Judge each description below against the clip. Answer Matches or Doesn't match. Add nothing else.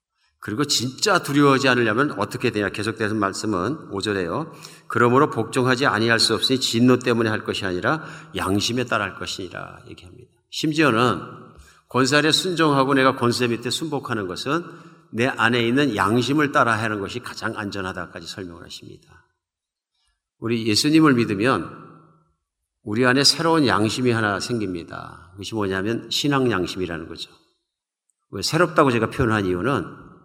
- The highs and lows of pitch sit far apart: Doesn't match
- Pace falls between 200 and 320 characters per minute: Doesn't match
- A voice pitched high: Doesn't match